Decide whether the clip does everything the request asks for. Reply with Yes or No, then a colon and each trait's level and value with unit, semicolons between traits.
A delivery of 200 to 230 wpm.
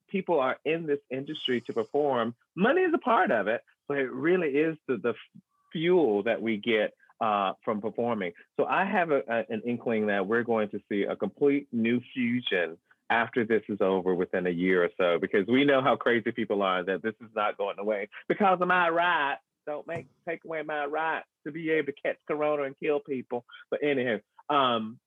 Yes: fast, 205 wpm